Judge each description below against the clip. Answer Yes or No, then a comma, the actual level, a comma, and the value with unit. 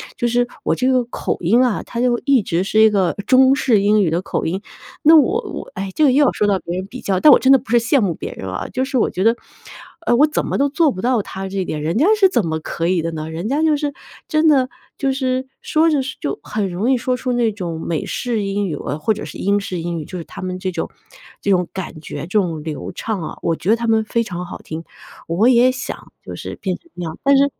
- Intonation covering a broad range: Yes, wide, 6.2 semitones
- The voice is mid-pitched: No, high, 215 Hz